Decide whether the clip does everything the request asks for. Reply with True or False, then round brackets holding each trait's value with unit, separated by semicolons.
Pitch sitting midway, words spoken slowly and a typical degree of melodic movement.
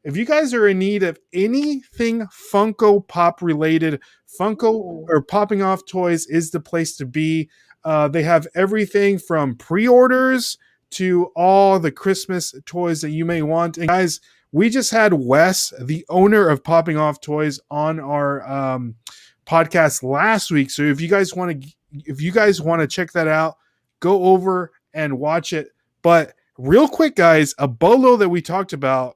False (170 Hz; 170 wpm; 4.3 semitones)